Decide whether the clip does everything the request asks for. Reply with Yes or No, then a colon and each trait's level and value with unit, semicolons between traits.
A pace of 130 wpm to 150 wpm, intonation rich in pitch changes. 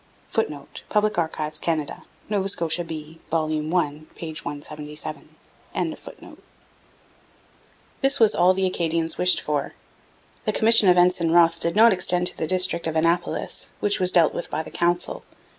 No: average, 145 wpm; average, 2.7 semitones